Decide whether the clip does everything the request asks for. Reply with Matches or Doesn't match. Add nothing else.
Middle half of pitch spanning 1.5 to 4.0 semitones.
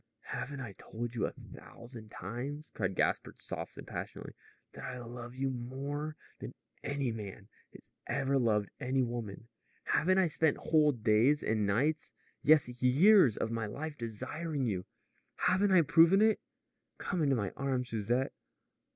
Doesn't match